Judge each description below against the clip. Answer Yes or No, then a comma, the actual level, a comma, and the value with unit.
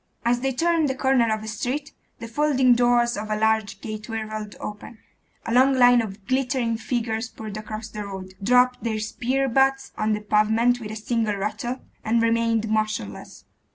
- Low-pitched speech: No, high, 230 Hz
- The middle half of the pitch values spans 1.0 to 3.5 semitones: Yes, narrow, 2.5 semitones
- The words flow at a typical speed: Yes, average, 180 wpm